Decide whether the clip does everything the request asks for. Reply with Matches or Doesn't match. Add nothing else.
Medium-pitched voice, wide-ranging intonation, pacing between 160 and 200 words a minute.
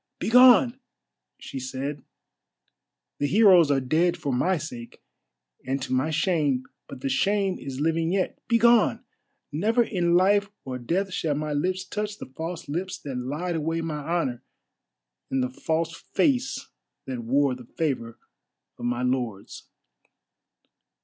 Doesn't match